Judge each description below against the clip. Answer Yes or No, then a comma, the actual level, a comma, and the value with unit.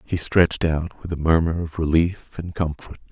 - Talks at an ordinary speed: Yes, average, 195 wpm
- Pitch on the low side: Yes, very low, 80 Hz